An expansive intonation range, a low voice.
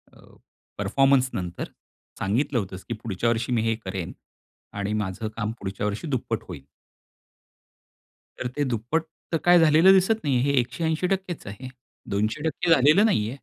Yes: wide, 7.1 semitones; low, 120 Hz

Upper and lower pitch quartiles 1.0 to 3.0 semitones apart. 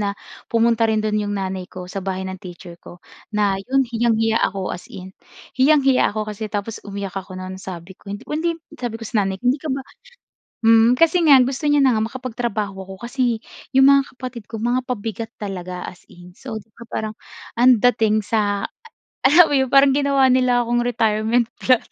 No: average, 4.3 semitones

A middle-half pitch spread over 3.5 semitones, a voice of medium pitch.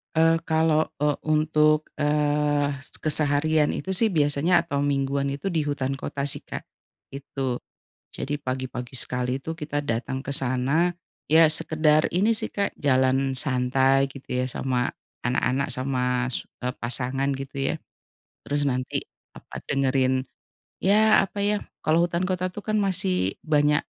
No: average, 3.1 semitones; medium, 145 Hz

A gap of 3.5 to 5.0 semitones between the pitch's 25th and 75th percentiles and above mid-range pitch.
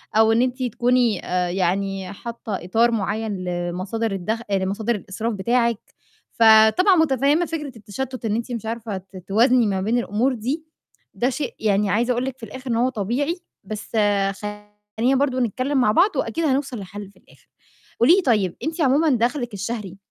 Yes: average, 4.0 semitones; high, 230 Hz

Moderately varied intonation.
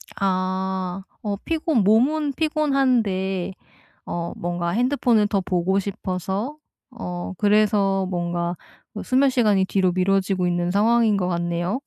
Yes: average, 4.1 semitones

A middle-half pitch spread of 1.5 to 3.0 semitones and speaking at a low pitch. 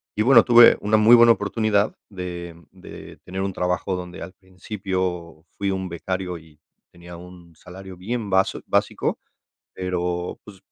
Yes: narrow, 2.5 semitones; very low, 95 Hz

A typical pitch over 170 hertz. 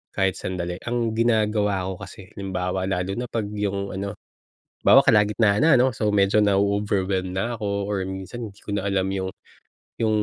No: low, 100 Hz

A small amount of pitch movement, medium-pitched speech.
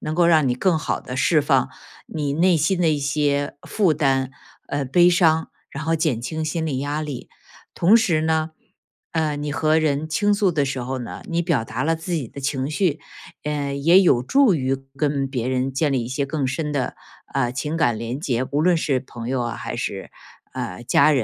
No: average, 3.3 semitones; medium, 150 Hz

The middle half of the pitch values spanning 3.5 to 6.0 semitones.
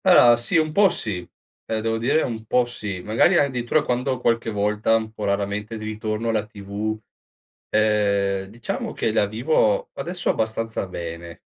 No: average, 2.7 semitones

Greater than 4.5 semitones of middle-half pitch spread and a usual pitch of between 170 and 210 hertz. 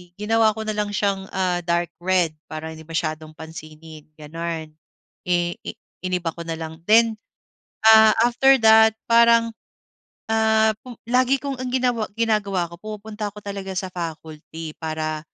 Yes: average, 5.2 semitones; high, 190 Hz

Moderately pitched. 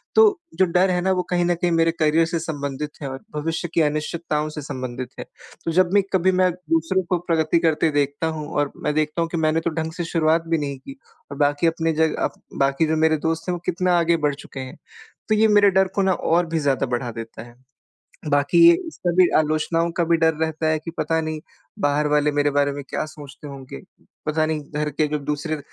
Yes: medium, 160 Hz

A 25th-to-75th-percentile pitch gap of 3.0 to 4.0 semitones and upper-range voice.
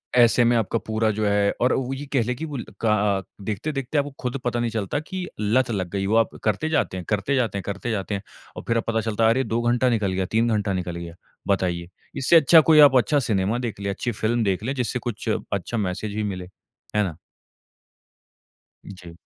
No: average, 3.6 semitones; low, 110 Hz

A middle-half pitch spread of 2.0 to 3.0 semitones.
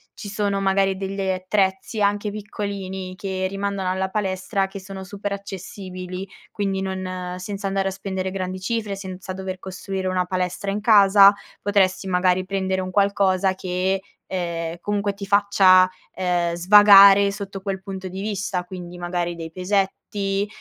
No: narrow, 1.3 semitones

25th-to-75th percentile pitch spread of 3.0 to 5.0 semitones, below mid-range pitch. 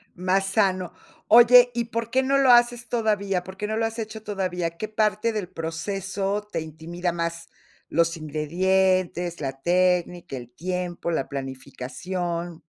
No: average, 4.1 semitones; medium, 185 Hz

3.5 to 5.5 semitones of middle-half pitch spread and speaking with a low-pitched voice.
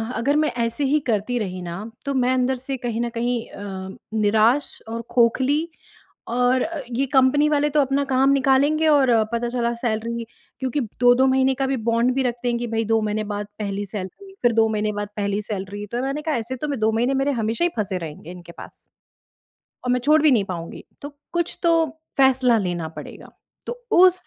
No: average, 4.1 semitones; high, 245 Hz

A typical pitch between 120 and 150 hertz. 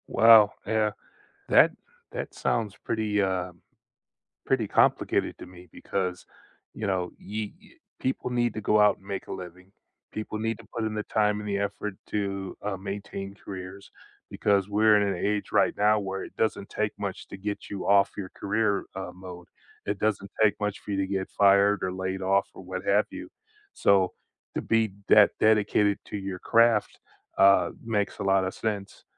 No: low, 100 Hz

